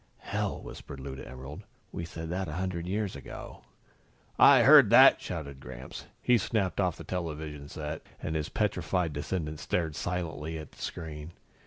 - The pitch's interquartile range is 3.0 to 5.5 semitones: Yes, average, 3.3 semitones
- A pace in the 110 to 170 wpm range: Yes, average, 165 wpm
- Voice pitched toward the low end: Yes, very low, 80 Hz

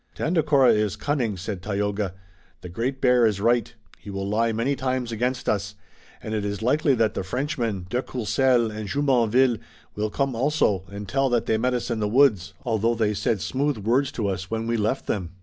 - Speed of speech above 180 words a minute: Yes, average, 200 wpm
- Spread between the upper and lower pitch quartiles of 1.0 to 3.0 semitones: No, average, 3.8 semitones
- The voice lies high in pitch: No, low, 115 Hz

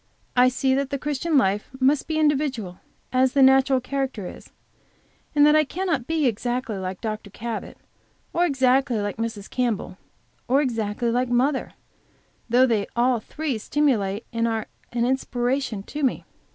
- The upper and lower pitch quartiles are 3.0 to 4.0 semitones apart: Yes, average, 3.4 semitones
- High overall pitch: Yes, very high, 255 Hz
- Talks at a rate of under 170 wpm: Yes, average, 155 wpm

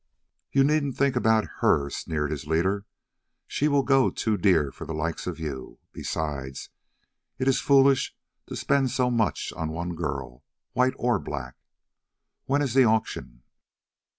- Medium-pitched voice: No, low, 105 Hz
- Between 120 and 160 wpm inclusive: Yes, average, 150 wpm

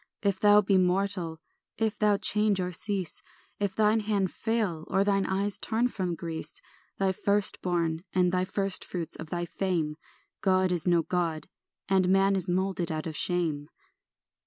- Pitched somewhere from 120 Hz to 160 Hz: No, high, 190 Hz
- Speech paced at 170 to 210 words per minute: No, average, 160 wpm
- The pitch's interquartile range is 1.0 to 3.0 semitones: Yes, narrow, 2.6 semitones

